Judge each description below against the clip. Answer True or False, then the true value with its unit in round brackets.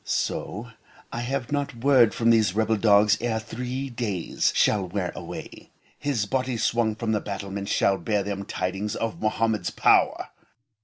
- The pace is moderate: True (155 wpm)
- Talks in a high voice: False (110 Hz)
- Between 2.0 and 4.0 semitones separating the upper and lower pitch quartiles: True (3.0 semitones)